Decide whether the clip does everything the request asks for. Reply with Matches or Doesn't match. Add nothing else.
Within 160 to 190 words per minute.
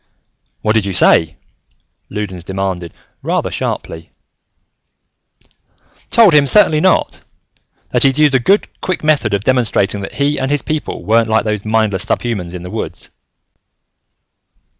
Doesn't match